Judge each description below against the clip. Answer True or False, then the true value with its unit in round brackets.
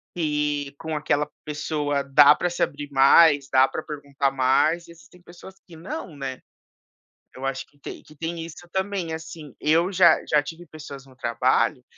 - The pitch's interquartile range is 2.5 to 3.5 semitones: True (3.1 semitones)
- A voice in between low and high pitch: True (150 Hz)